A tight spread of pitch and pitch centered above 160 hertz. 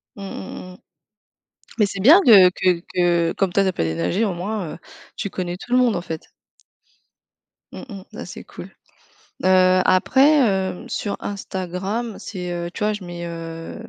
No: average, 3.0 semitones; medium, 185 Hz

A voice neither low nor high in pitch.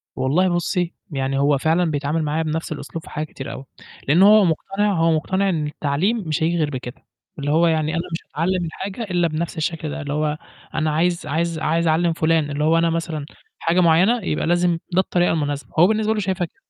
Yes: medium, 165 Hz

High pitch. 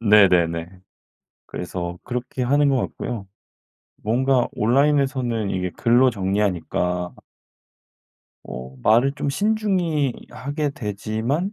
No: low, 120 Hz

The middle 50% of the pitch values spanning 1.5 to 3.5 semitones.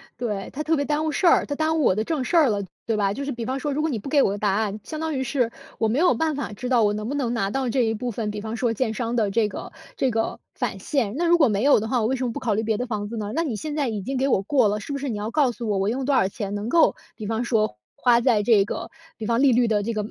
No: average, 4.5 semitones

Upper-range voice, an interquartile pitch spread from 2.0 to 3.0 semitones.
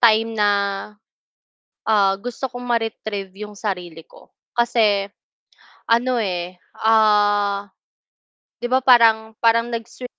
Yes: high, 220 Hz; narrow, 2.5 semitones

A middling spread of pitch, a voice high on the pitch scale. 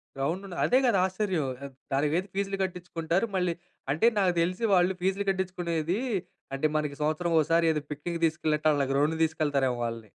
No: average, 3.7 semitones; medium, 170 Hz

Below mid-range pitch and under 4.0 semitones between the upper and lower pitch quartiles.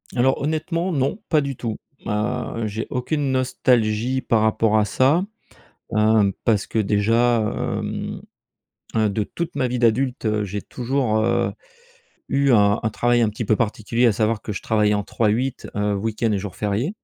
Yes: low, 115 Hz; average, 3.4 semitones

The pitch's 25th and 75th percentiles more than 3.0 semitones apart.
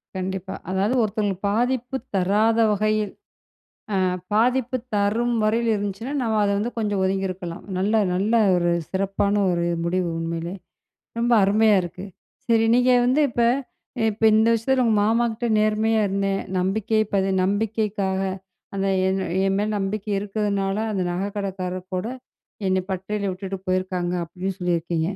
No: average, 2.7 semitones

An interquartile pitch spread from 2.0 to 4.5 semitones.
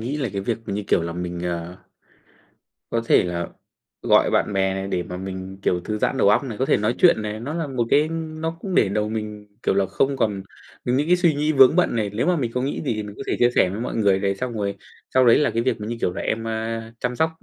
No: average, 5.2 semitones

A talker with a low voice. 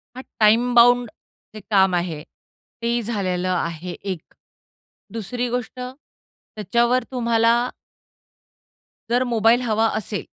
No: high, 230 Hz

